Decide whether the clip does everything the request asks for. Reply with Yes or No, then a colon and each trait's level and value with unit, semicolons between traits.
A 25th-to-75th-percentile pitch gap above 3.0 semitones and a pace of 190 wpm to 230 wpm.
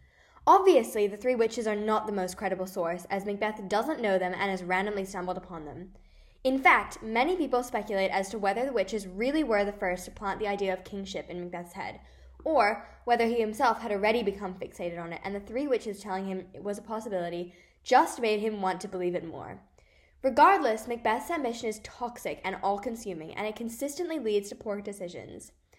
Yes: average, 3.6 semitones; average, 200 wpm